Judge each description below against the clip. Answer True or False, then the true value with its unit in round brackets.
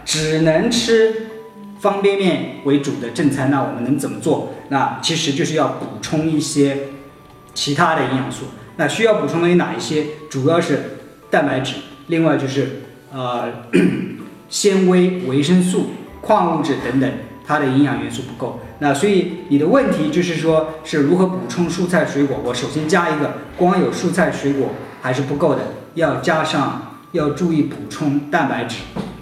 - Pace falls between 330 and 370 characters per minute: False (245 characters per minute)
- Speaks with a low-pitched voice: False (155 Hz)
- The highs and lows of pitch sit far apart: False (3.9 semitones)